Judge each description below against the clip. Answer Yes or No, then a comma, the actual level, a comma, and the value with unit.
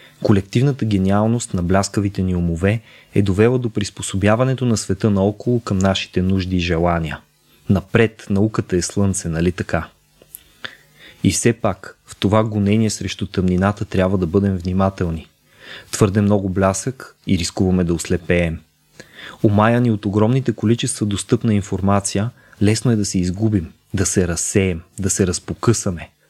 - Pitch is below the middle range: Yes, low, 100 Hz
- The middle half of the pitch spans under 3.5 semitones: Yes, average, 2.9 semitones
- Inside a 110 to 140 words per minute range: Yes, average, 135 wpm